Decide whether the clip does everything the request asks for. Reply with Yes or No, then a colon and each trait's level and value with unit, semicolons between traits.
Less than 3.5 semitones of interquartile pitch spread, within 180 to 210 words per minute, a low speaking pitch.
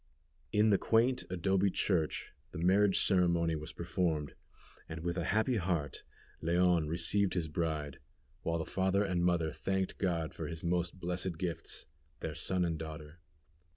No: average, 2.7 semitones; average, 155 wpm; very low, 85 Hz